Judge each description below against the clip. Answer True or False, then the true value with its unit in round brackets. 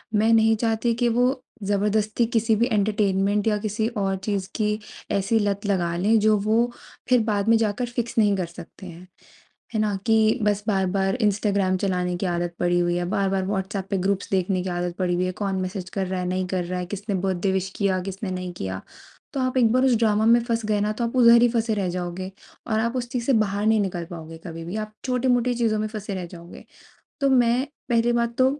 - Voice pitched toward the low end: False (205 Hz)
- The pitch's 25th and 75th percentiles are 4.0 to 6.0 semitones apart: False (3.3 semitones)